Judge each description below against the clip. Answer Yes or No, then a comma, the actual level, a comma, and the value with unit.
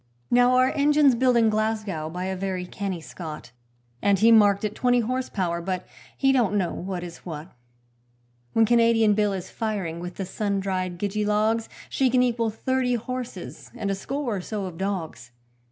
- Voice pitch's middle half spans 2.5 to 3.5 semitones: No, average, 4.3 semitones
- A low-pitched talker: No, high, 210 Hz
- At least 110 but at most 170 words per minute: No, average, 185 wpm